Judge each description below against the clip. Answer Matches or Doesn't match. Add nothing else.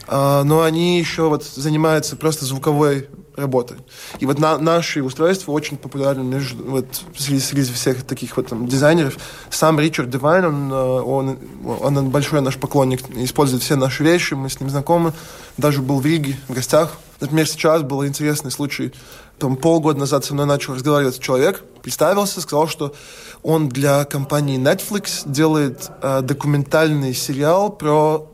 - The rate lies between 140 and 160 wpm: Matches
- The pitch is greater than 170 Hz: Doesn't match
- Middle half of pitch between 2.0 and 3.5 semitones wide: Matches